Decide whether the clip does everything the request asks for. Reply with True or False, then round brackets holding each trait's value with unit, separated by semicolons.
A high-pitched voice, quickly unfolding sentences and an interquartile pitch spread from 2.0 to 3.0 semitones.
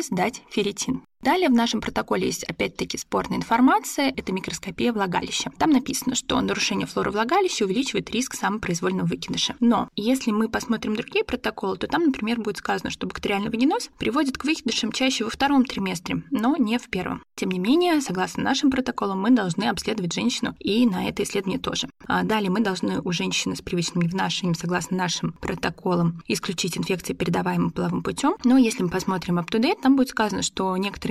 False (220 Hz; 175 wpm; 5.1 semitones)